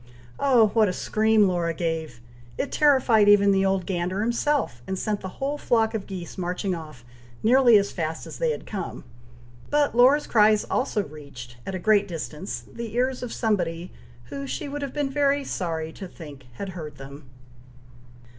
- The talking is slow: No, average, 175 wpm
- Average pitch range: No, wide, 6.4 semitones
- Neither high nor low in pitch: No, high, 200 Hz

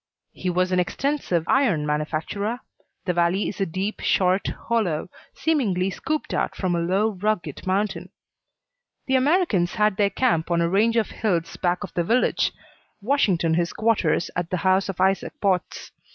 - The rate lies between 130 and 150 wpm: No, average, 165 wpm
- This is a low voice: No, high, 190 Hz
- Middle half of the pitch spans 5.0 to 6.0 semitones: No, average, 3.8 semitones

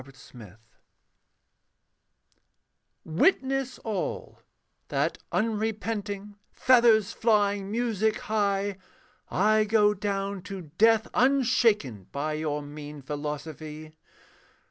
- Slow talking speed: Yes, slow, 80 wpm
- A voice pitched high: Yes, high, 205 Hz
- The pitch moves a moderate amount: No, wide, 6.2 semitones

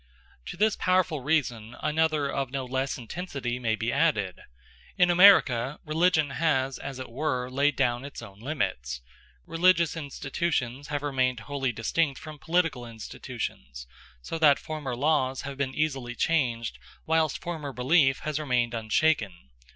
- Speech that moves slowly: No, average, 145 wpm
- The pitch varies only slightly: No, average, 4.4 semitones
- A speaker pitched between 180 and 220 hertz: No, medium, 140 Hz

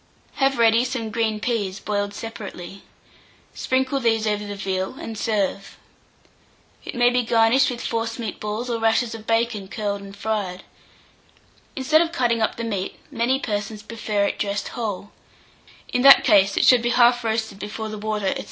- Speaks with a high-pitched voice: Yes, high, 225 Hz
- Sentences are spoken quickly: No, average, 170 wpm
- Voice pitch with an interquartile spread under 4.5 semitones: Yes, narrow, 2.6 semitones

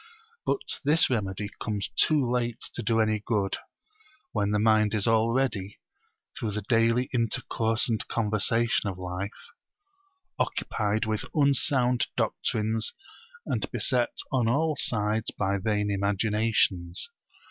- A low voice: Yes, low, 110 Hz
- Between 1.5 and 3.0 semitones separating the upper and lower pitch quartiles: Yes, narrow, 2.5 semitones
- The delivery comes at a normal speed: No, slow, 120 wpm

